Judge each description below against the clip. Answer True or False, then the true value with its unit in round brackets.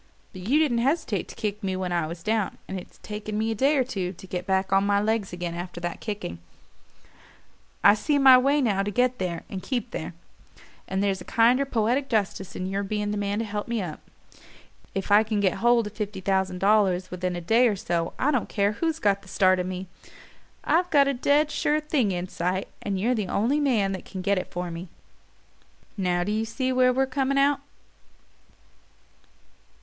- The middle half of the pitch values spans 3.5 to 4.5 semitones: False (4.9 semitones)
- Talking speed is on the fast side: True (210 wpm)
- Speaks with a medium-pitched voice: False (205 Hz)